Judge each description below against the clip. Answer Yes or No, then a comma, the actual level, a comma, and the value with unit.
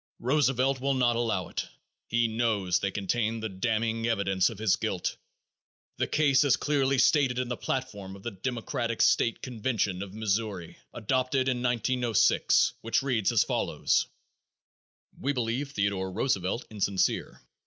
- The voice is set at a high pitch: No, low, 115 Hz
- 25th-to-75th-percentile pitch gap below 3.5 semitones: No, average, 4.2 semitones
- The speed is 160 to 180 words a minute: No, average, 145 wpm